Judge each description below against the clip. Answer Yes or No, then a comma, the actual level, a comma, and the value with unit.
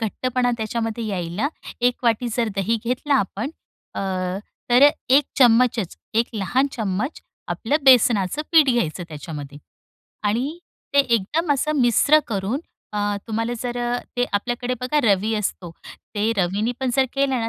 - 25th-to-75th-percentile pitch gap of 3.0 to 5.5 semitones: Yes, average, 3.7 semitones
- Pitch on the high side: Yes, high, 235 Hz